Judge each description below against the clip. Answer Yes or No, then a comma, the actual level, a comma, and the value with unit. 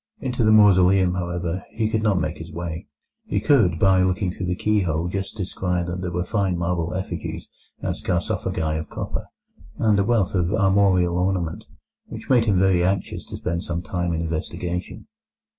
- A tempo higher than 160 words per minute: Yes, average, 175 wpm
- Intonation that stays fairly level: Yes, narrow, 2.2 semitones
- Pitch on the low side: Yes, very low, 90 Hz